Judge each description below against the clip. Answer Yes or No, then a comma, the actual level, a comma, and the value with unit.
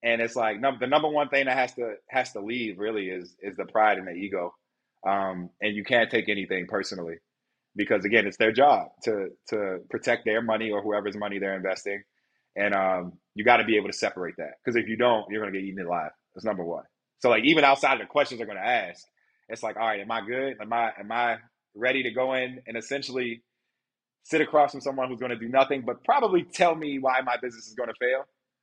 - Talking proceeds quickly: Yes, fast, 240 wpm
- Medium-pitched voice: No, low, 115 Hz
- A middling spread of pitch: Yes, average, 3.8 semitones